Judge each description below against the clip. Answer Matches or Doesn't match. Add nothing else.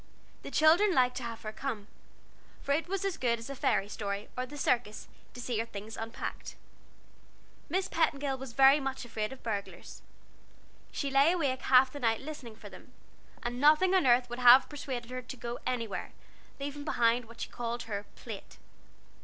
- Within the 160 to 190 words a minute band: Matches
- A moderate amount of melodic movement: Matches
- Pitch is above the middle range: Matches